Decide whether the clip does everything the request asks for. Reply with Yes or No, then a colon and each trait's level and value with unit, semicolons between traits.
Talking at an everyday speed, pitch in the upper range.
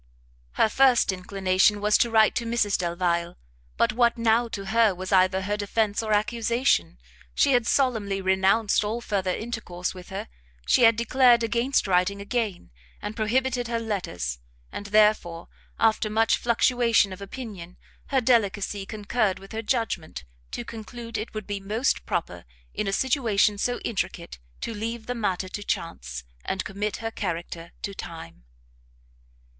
Yes: average, 155 wpm; high, 210 Hz